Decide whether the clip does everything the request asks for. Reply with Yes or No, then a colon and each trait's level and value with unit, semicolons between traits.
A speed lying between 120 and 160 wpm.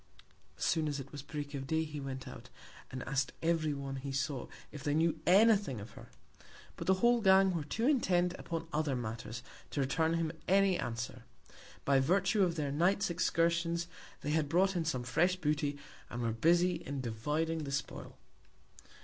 No: average, 185 wpm